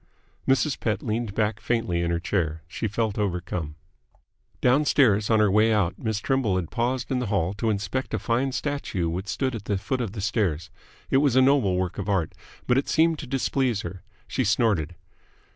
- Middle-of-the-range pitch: No, low, 110 Hz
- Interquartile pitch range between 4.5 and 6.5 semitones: Yes, average, 5.1 semitones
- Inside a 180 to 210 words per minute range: Yes, average, 195 wpm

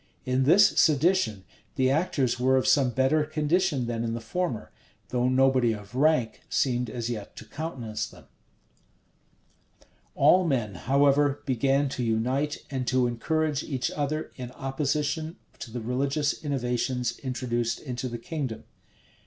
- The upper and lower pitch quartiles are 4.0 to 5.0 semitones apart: No, average, 3.3 semitones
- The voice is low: Yes, low, 130 Hz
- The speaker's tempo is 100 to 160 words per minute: Yes, average, 140 wpm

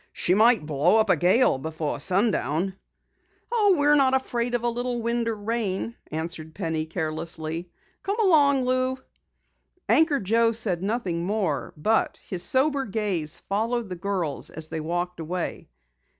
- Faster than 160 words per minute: No, average, 150 wpm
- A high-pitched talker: Yes, high, 200 Hz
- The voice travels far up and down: Yes, wide, 6.4 semitones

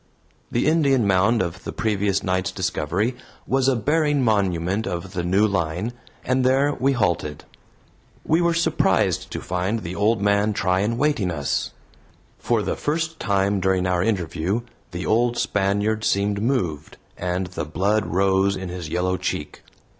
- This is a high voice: No, low, 100 Hz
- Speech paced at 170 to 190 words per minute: No, average, 155 wpm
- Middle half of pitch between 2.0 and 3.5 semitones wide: No, average, 4.3 semitones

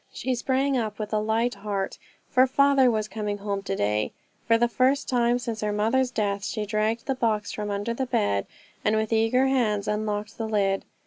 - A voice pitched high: Yes, high, 220 Hz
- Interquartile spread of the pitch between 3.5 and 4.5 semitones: No, average, 2.8 semitones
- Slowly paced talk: No, average, 200 wpm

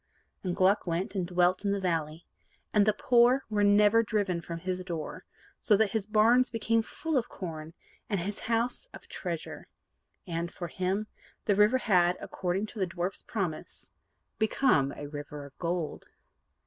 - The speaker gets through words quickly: No, average, 165 wpm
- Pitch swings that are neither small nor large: Yes, average, 3.8 semitones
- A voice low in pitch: No, high, 190 Hz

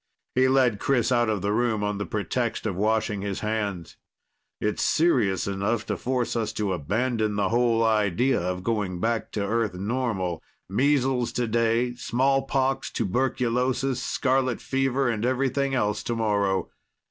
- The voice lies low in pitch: Yes, low, 115 Hz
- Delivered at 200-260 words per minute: No, average, 145 wpm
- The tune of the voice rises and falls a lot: No, average, 3.7 semitones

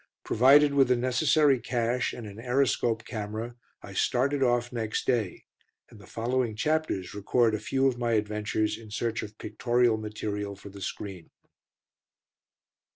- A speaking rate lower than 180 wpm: Yes, average, 150 wpm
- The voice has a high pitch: No, low, 115 Hz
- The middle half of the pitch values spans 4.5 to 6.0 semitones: No, average, 3.1 semitones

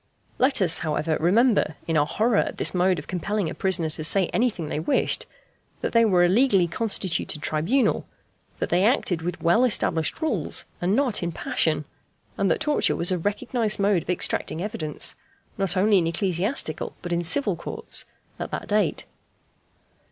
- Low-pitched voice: No, medium, 185 Hz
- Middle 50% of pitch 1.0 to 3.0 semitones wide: No, average, 4.4 semitones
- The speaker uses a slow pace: No, average, 175 wpm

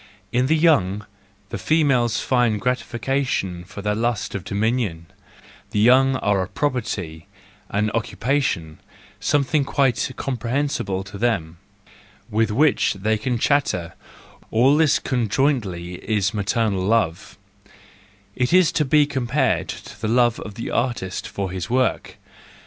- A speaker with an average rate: No, slow, 130 wpm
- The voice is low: Yes, low, 115 Hz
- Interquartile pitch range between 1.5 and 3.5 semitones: No, average, 4.9 semitones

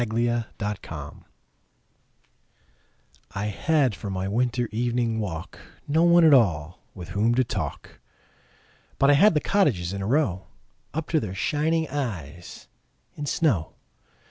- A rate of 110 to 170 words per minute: Yes, slow, 135 wpm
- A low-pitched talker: Yes, low, 120 Hz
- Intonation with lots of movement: Yes, wide, 7.3 semitones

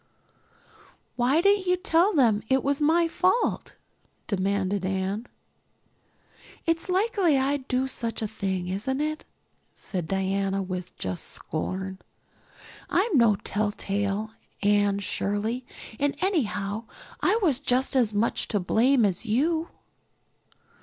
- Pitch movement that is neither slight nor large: No, wide, 6.9 semitones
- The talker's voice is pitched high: Yes, high, 230 Hz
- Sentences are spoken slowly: Yes, slow, 120 wpm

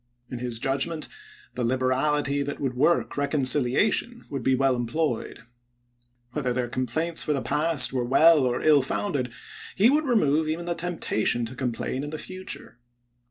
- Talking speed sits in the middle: Yes, average, 160 wpm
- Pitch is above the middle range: No, medium, 140 Hz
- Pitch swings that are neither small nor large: Yes, average, 4.1 semitones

